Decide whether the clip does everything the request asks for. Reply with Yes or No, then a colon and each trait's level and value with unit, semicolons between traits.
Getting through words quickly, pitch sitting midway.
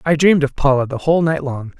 Yes: fast, 270 wpm; medium, 170 Hz